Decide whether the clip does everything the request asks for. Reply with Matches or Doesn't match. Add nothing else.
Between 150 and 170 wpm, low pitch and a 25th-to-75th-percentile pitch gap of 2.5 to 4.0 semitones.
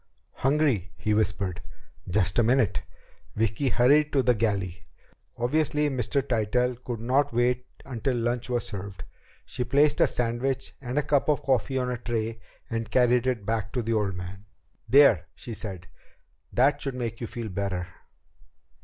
Matches